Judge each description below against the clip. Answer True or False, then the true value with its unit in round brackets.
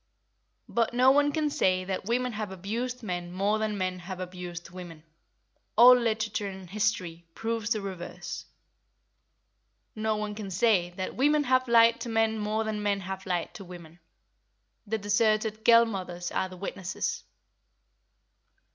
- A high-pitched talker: True (210 Hz)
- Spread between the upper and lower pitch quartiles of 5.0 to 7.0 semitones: False (3.6 semitones)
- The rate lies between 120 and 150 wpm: True (145 wpm)